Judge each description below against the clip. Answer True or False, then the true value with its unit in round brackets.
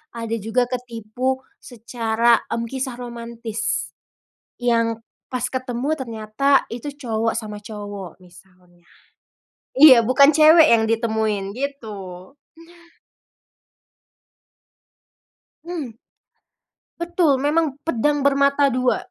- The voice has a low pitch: False (240 Hz)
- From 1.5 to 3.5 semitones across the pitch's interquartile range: False (3.9 semitones)